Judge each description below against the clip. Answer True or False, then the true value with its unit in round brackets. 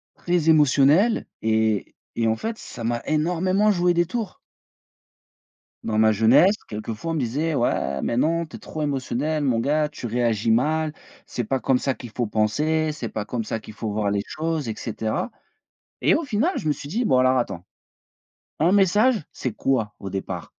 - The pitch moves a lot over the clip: True (6.5 semitones)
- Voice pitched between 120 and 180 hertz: True (135 Hz)